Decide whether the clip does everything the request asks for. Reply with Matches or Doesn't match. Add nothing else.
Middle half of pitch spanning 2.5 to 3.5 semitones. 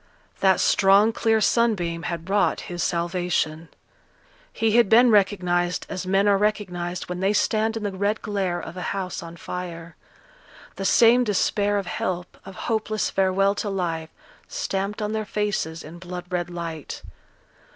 Matches